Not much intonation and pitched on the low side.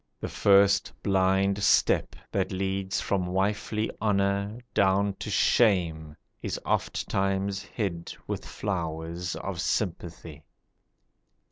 Yes: narrow, 2.1 semitones; very low, 95 Hz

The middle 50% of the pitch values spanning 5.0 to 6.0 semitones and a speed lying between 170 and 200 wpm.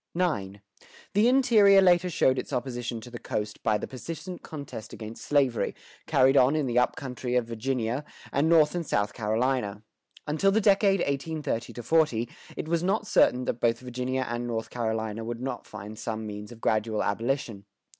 Yes: wide, 5.6 semitones; average, 175 wpm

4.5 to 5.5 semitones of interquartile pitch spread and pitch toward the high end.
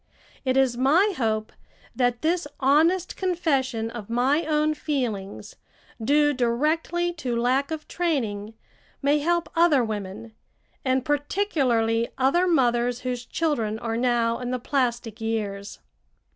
Yes: average, 4.8 semitones; very high, 255 Hz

